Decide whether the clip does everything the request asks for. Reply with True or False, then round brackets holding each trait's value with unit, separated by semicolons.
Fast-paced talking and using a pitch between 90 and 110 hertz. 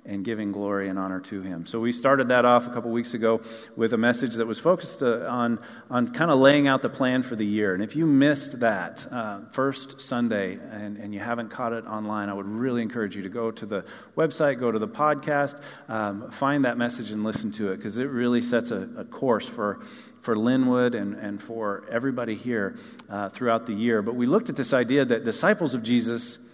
False (225 wpm; 120 Hz)